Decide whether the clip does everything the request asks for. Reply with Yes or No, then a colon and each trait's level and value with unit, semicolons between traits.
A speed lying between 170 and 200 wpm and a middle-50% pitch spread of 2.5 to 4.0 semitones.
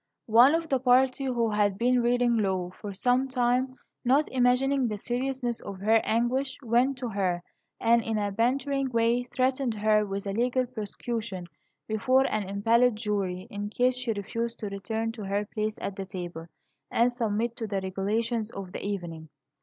Yes: average, 175 wpm; average, 3.6 semitones